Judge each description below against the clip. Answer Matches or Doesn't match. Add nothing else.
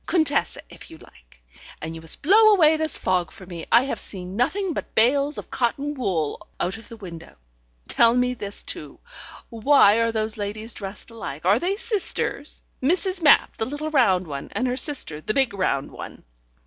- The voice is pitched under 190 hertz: Doesn't match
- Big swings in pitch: Matches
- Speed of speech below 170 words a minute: Doesn't match